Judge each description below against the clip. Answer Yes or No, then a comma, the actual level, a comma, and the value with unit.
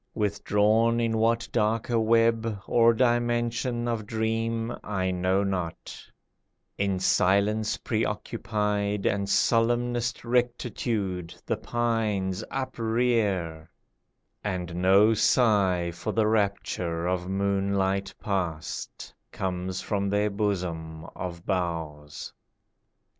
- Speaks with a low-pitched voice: Yes, low, 105 Hz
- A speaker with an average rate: No, slow, 95 wpm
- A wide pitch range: No, average, 3.5 semitones